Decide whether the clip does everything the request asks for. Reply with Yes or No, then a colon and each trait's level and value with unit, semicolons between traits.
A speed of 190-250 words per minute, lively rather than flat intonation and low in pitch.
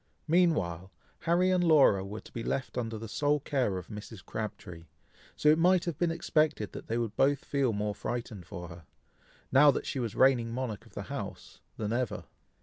Yes: average, 195 wpm; wide, 6.1 semitones; low, 120 Hz